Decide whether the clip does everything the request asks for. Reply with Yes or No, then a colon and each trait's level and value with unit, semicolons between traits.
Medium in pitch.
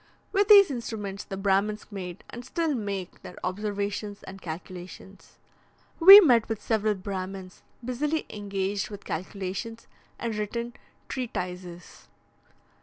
No: high, 205 Hz